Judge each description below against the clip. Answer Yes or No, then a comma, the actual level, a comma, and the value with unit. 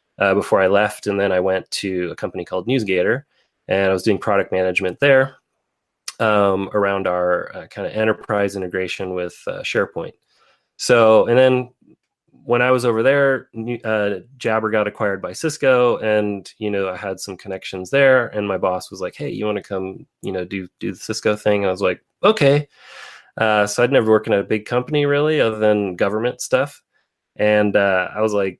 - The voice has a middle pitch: No, low, 105 Hz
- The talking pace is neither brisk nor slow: Yes, average, 195 wpm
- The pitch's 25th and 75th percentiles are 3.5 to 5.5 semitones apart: Yes, average, 4.1 semitones